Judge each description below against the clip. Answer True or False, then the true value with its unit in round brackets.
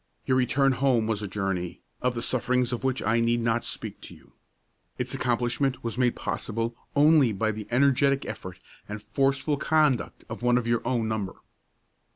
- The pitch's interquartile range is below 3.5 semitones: True (2.9 semitones)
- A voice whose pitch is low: True (120 Hz)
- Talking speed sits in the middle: True (180 wpm)